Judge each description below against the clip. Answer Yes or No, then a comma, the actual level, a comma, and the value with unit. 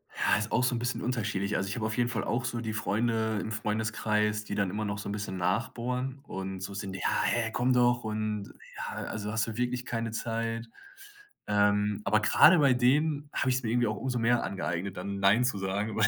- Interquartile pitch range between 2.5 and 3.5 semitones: Yes, average, 2.9 semitones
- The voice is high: No, low, 110 Hz